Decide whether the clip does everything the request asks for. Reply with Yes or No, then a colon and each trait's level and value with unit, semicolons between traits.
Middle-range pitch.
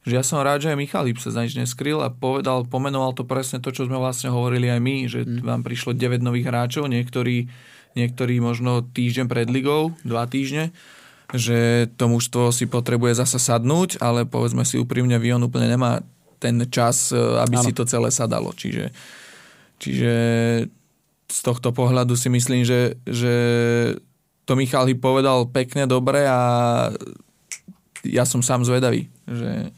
No: low, 125 Hz